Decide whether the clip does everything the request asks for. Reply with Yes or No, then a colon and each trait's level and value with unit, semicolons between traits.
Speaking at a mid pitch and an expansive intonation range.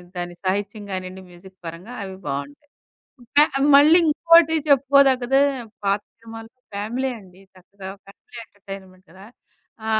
No: high, 200 Hz; wide, 6.0 semitones